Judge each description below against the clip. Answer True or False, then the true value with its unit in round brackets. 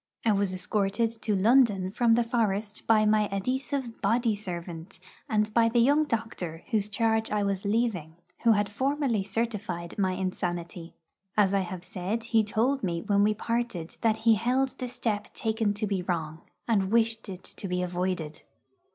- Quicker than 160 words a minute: True (170 wpm)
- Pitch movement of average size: True (3.5 semitones)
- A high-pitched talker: True (210 Hz)